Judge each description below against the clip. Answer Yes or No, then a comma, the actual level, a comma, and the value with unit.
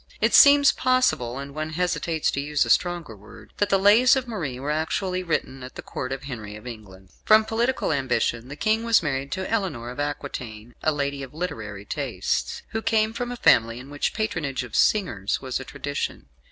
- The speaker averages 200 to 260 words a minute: Yes, fast, 205 wpm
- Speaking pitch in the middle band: Yes, medium, 145 Hz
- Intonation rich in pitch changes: Yes, wide, 8.1 semitones